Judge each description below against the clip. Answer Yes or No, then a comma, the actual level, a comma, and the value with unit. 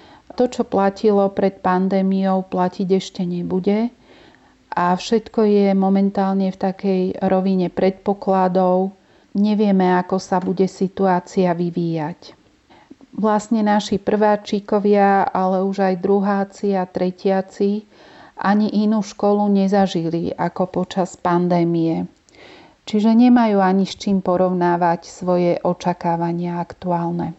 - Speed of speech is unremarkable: No, slow, 105 wpm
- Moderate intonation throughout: No, narrow, 2.1 semitones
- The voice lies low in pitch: No, high, 190 Hz